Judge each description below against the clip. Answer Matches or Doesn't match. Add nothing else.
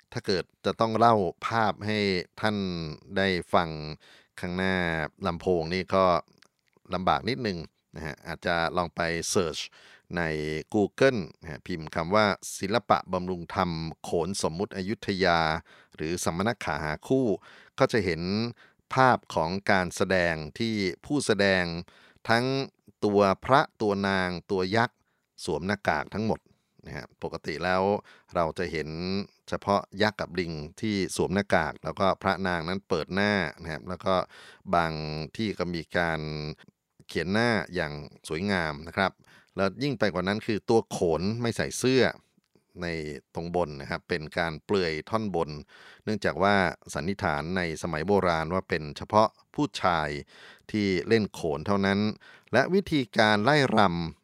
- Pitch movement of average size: Matches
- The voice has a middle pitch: Doesn't match